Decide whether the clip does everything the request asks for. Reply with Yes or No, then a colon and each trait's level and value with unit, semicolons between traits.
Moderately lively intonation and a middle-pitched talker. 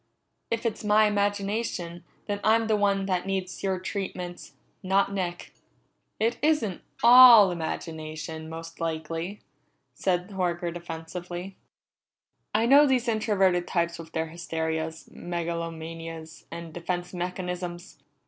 Yes: average, 3.5 semitones; medium, 180 Hz